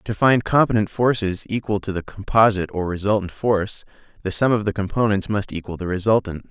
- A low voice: Yes, low, 100 Hz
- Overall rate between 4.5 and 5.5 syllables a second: No, 5.9 syllables/s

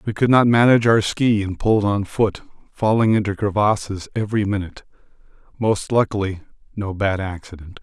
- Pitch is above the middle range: No, low, 105 Hz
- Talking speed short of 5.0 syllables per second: No, 5.6 syllables/s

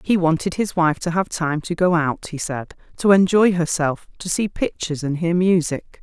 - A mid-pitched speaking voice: Yes, medium, 170 Hz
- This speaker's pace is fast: Yes, fast, 210 wpm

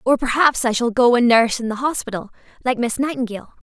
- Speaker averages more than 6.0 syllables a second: Yes, 6.4 syllables/s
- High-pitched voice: Yes, high, 240 Hz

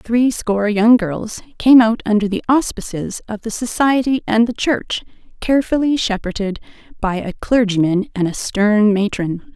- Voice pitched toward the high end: Yes, high, 220 Hz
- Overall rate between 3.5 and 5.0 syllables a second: Yes, 4.6 syllables/s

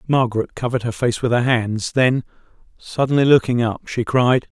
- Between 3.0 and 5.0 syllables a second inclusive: No, 5.2 syllables/s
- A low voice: Yes, low, 120 Hz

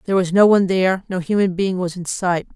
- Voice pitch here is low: No, medium, 185 Hz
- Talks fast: Yes, fast, 260 wpm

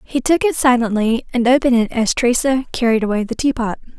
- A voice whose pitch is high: Yes, high, 245 Hz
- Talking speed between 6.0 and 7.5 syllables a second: Yes, 6.1 syllables/s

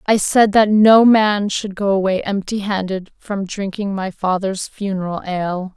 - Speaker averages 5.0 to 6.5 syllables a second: No, 4.3 syllables/s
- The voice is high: Yes, high, 200 Hz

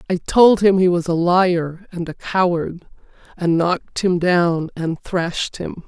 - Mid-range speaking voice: Yes, medium, 175 Hz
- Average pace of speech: Yes, average, 175 wpm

